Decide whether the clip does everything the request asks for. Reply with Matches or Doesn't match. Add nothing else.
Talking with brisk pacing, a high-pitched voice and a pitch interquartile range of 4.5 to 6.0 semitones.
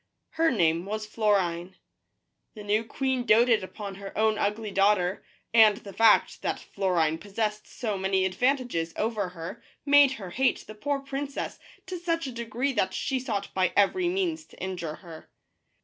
Doesn't match